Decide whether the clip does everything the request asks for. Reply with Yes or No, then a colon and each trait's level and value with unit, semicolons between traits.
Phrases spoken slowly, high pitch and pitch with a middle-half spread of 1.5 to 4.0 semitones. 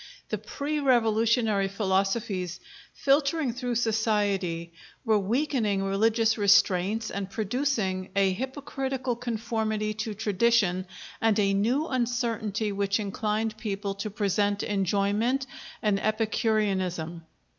Yes: slow, 100 wpm; high, 215 Hz; average, 3.0 semitones